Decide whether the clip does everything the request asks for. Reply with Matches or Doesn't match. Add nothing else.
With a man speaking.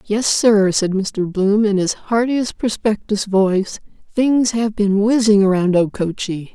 Doesn't match